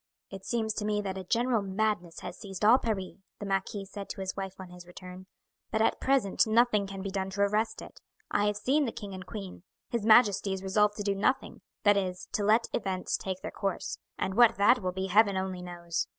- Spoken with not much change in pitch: Yes, narrow, 2.3 semitones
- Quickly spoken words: Yes, fast, 225 wpm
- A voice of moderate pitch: No, high, 200 Hz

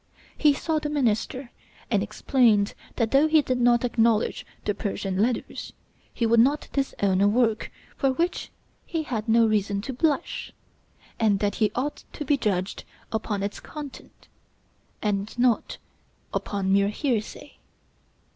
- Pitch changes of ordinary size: Yes, average, 4.7 semitones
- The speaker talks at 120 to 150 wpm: Yes, average, 145 wpm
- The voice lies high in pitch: Yes, high, 230 Hz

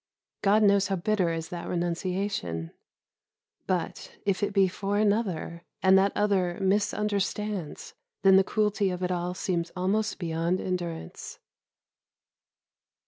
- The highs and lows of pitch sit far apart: No, average, 2.7 semitones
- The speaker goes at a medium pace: No, slow, 125 wpm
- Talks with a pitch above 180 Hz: Yes, high, 190 Hz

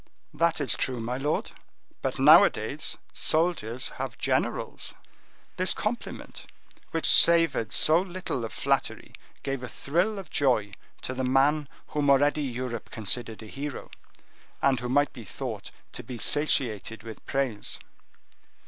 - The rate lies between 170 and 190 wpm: No, slow, 135 wpm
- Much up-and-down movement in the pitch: No, average, 4.2 semitones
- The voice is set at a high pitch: No, low, 135 Hz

